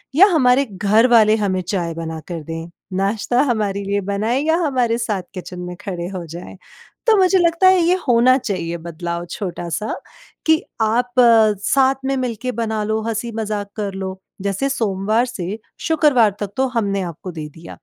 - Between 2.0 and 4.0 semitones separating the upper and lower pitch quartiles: No, average, 4.9 semitones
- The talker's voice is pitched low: No, high, 215 Hz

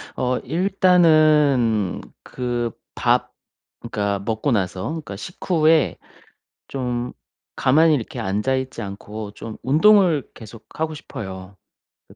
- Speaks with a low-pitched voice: Yes, low, 125 Hz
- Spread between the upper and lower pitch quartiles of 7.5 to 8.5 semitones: No, wide, 6.4 semitones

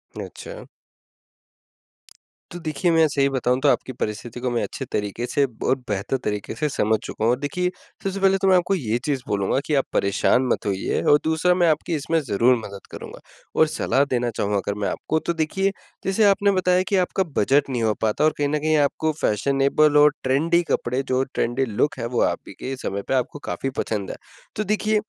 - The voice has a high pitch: No, medium, 140 Hz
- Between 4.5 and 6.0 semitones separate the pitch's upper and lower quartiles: Yes, wide, 5.4 semitones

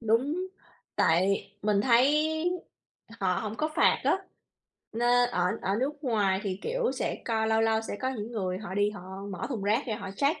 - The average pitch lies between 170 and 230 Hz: Yes, high, 220 Hz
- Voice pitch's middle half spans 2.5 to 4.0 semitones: No, average, 4.8 semitones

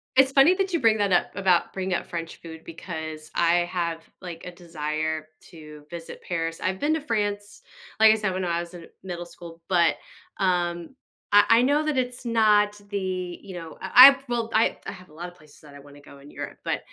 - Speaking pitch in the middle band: Yes, medium, 180 Hz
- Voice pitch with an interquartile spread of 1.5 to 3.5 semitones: No, average, 4.3 semitones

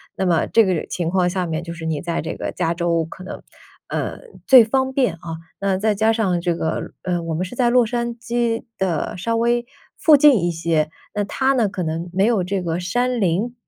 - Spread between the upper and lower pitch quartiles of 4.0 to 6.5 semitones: Yes, wide, 5.6 semitones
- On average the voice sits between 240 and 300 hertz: No, high, 190 Hz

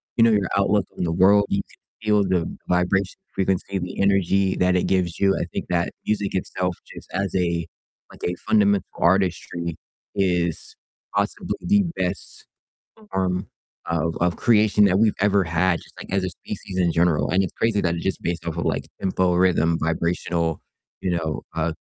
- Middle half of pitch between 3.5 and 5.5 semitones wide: No, narrow, 2.4 semitones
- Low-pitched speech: Yes, very low, 95 Hz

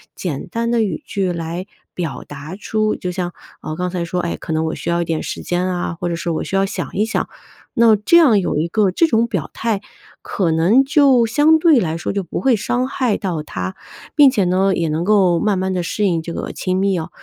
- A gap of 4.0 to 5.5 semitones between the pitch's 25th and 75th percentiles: Yes, average, 4.7 semitones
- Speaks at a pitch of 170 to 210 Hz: Yes, medium, 185 Hz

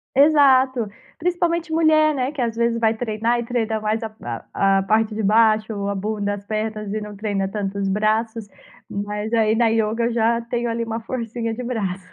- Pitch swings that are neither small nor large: No, narrow, 2.1 semitones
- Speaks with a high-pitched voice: Yes, high, 225 Hz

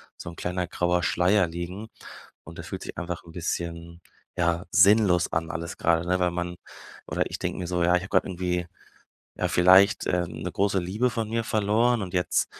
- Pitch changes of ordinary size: No, narrow, 2.2 semitones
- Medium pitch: No, very low, 90 Hz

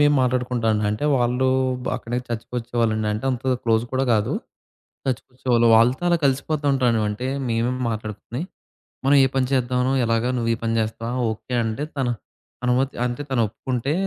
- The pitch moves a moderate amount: No, narrow, 2.3 semitones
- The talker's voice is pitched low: Yes, low, 120 Hz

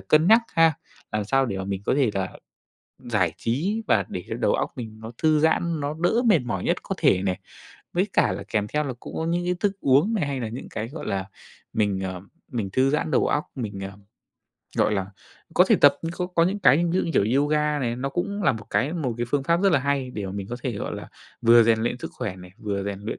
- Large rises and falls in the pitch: Yes, wide, 7.4 semitones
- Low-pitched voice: Yes, low, 130 Hz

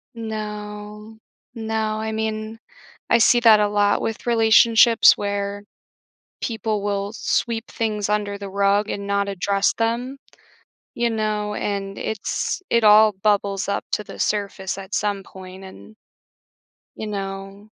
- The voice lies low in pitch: No, high, 210 Hz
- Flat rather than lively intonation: Yes, narrow, 1.6 semitones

